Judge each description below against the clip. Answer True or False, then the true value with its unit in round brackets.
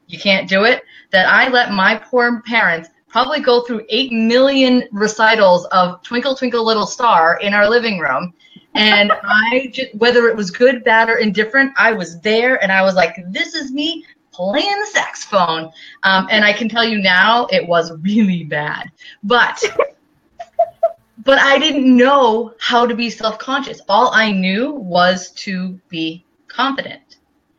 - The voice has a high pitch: True (230 Hz)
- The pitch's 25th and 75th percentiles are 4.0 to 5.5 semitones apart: True (5.1 semitones)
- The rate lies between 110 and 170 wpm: True (165 wpm)